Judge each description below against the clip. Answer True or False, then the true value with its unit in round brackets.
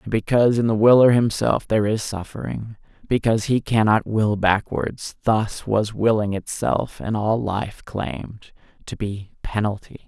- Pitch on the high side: False (110 Hz)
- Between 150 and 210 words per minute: False (135 wpm)